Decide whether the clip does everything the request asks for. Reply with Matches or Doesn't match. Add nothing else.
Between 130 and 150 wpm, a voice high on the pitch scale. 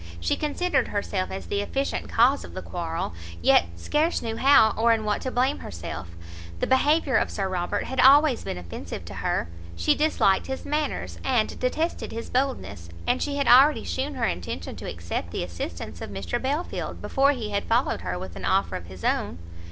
Doesn't match